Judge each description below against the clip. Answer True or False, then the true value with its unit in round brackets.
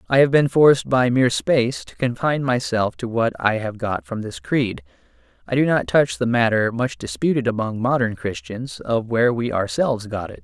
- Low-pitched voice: True (120 Hz)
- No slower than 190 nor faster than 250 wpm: True (200 wpm)